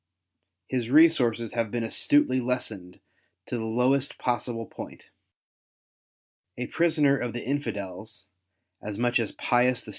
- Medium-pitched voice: No, low, 120 Hz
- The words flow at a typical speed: No, slow, 125 wpm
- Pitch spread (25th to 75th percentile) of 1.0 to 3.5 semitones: Yes, narrow, 2.6 semitones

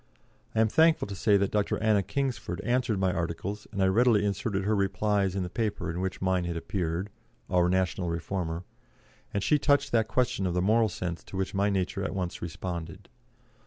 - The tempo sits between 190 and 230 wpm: Yes, average, 200 wpm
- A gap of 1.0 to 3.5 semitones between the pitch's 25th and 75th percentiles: Yes, average, 3.0 semitones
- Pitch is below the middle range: Yes, very low, 95 Hz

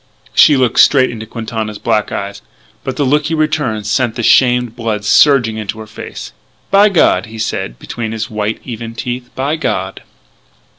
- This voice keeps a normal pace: Yes, average, 170 wpm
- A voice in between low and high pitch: No, low, 115 Hz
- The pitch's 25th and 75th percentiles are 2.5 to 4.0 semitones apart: Yes, average, 3.4 semitones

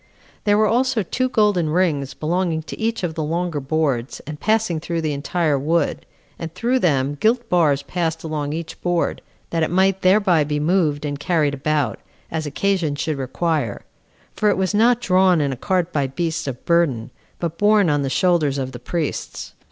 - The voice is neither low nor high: Yes, medium, 165 Hz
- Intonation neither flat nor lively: Yes, average, 4.2 semitones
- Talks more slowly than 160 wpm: No, average, 185 wpm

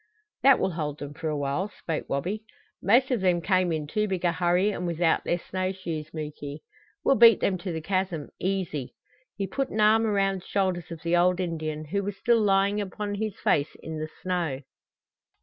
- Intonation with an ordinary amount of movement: Yes, average, 3.9 semitones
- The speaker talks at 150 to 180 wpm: No, average, 200 wpm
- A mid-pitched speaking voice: Yes, medium, 180 Hz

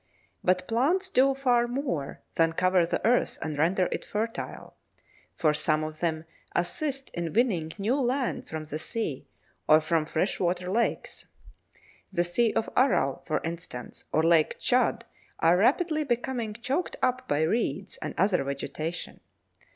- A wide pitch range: Yes, wide, 7.3 semitones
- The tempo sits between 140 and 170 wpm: Yes, average, 145 wpm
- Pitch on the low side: No, medium, 185 Hz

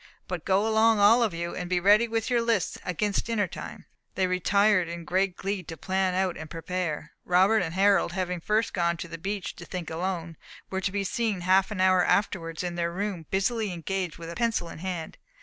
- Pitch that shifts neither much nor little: Yes, average, 3.0 semitones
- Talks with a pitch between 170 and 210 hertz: Yes, medium, 185 Hz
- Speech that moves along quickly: Yes, fast, 210 wpm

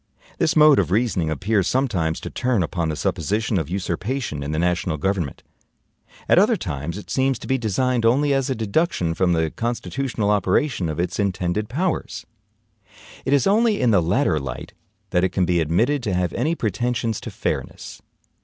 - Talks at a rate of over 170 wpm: Yes, average, 180 wpm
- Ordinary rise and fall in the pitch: No, wide, 6.8 semitones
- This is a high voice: No, low, 100 Hz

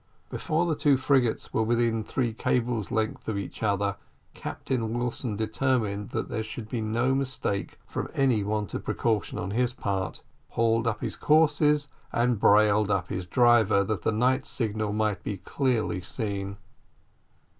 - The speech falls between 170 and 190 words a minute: No, average, 155 wpm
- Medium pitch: No, low, 110 Hz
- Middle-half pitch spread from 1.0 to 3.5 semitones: Yes, average, 3.2 semitones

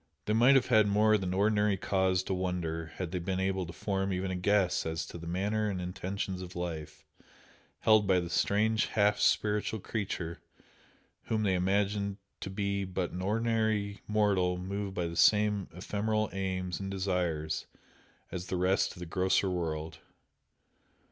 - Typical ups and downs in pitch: No, narrow, 2.3 semitones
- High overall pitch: No, very low, 95 Hz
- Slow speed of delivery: No, average, 165 wpm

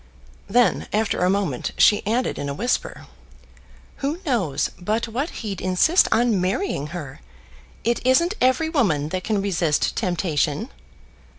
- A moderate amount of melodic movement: No, wide, 5.8 semitones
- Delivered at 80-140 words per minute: Yes, slow, 135 wpm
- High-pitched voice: Yes, high, 210 Hz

